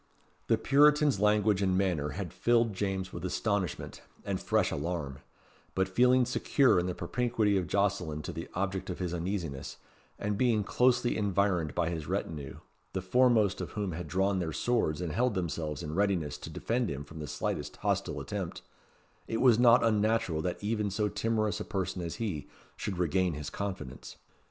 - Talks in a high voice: No, very low, 95 Hz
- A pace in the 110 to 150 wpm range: No, average, 175 wpm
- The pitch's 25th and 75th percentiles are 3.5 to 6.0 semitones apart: Yes, average, 4.4 semitones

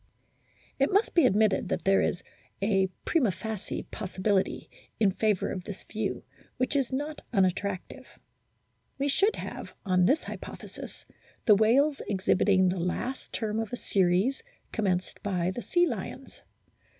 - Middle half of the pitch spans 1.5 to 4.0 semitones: No, wide, 5.6 semitones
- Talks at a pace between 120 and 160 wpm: Yes, average, 145 wpm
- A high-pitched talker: Yes, high, 210 Hz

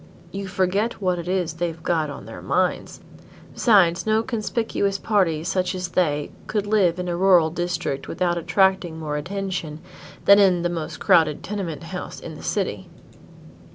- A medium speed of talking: Yes, average, 160 wpm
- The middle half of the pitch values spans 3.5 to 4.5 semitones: No, average, 3.0 semitones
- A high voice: No, medium, 180 Hz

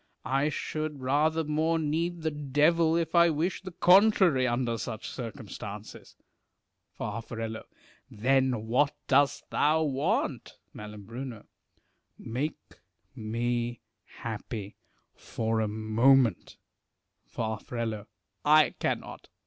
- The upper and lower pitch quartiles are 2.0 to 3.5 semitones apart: No, wide, 5.4 semitones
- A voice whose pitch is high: No, low, 135 Hz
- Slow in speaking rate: Yes, slow, 95 wpm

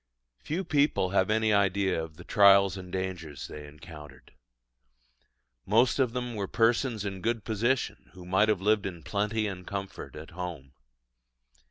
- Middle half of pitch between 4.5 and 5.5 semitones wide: No, average, 3.6 semitones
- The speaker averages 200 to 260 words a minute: No, average, 155 wpm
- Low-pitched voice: Yes, low, 100 Hz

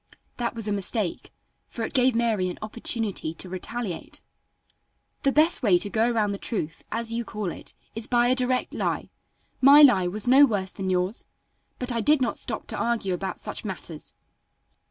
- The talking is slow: No, average, 185 wpm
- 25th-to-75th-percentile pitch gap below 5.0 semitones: Yes, average, 4.0 semitones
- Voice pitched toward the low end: No, high, 225 Hz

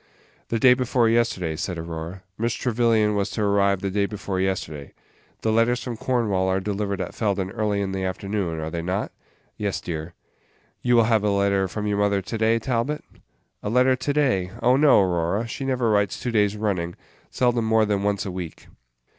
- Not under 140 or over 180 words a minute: No, average, 195 wpm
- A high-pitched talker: No, low, 105 Hz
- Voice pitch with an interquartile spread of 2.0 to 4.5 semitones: Yes, average, 3.5 semitones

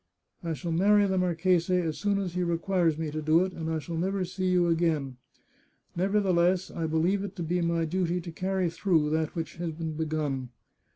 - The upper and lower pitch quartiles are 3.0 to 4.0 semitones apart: No, narrow, 2.4 semitones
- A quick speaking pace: Yes, fast, 215 wpm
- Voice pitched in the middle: Yes, medium, 170 Hz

